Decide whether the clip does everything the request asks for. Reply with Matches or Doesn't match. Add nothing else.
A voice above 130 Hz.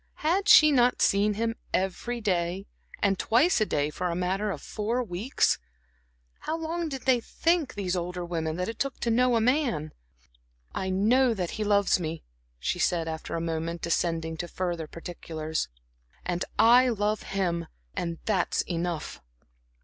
Matches